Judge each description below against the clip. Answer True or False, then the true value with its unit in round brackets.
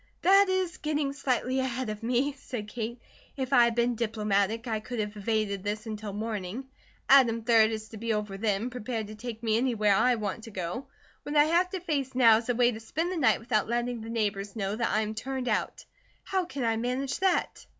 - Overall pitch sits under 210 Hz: False (230 Hz)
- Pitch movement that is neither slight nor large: True (3.3 semitones)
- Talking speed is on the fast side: True (220 wpm)